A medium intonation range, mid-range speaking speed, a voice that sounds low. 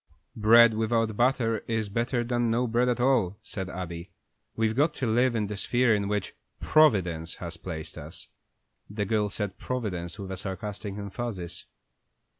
Yes: average, 3.7 semitones; average, 160 wpm; low, 110 Hz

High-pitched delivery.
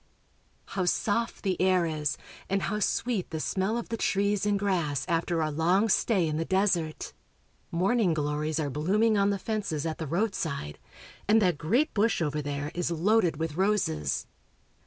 No: medium, 180 Hz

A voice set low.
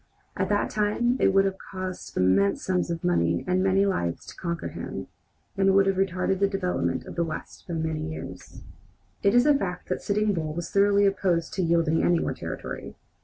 No: medium, 185 Hz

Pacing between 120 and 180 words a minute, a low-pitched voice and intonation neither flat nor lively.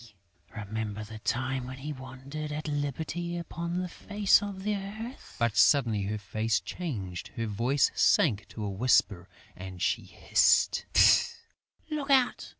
No: average, 145 wpm; low, 130 Hz; wide, 8.2 semitones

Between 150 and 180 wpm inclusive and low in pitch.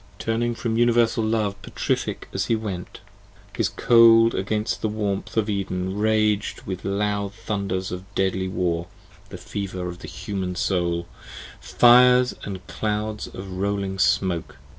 No: average, 140 wpm; low, 100 Hz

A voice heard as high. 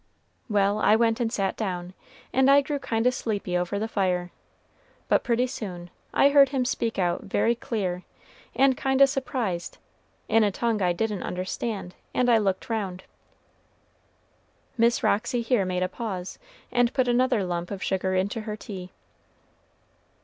Yes: high, 215 Hz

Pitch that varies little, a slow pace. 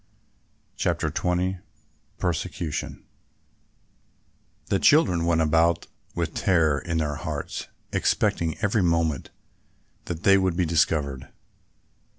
Yes: narrow, 2.3 semitones; slow, 100 wpm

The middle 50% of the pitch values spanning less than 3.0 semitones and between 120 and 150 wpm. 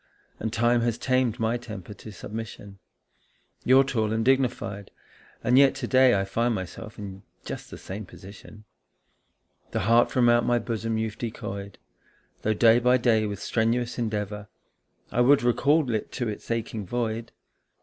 No: narrow, 2.4 semitones; average, 160 wpm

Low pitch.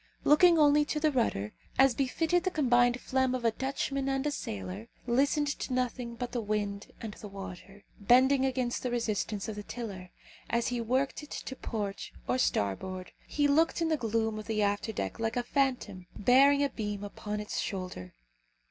No: high, 240 Hz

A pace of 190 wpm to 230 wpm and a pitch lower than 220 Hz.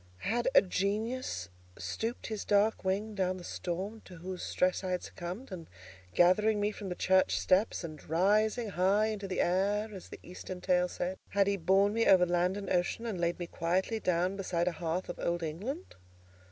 Yes: average, 195 wpm; high, 190 Hz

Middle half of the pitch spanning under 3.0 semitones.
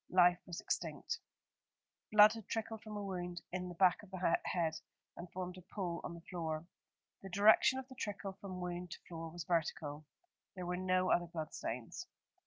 Yes: narrow, 2.5 semitones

